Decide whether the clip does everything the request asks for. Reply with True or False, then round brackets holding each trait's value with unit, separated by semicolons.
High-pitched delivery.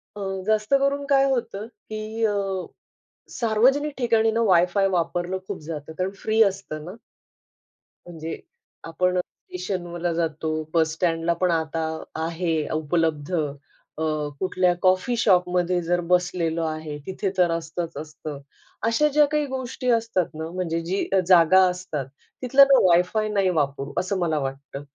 False (180 Hz)